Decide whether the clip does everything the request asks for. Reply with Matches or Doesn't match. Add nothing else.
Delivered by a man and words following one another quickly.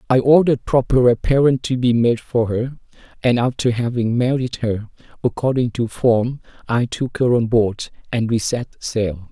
Doesn't match